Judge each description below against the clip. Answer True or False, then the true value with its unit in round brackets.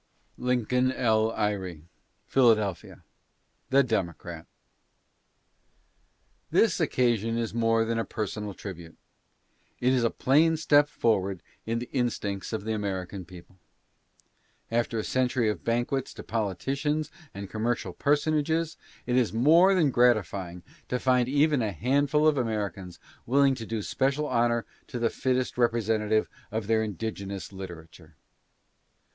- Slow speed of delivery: True (130 wpm)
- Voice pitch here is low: True (115 Hz)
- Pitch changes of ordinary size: True (4.1 semitones)